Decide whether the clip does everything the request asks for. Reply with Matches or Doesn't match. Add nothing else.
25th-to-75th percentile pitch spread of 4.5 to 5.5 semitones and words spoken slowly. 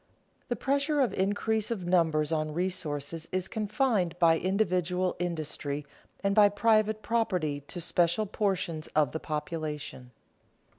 Matches